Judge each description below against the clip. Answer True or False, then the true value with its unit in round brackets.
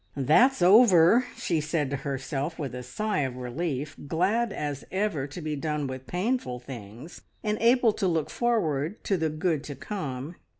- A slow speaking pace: False (170 wpm)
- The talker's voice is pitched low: False (155 Hz)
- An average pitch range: False (6.2 semitones)